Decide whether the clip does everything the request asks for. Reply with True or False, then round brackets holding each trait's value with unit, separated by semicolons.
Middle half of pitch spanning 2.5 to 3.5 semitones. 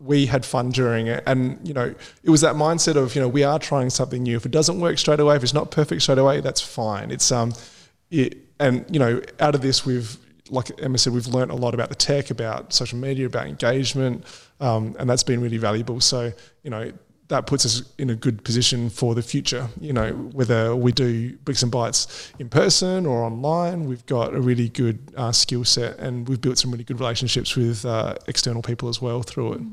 True (2.8 semitones)